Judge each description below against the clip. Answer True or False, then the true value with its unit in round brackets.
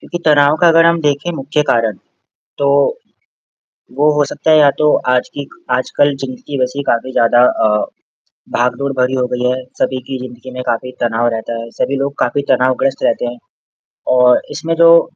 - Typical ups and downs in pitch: True (3.0 semitones)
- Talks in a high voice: False (130 Hz)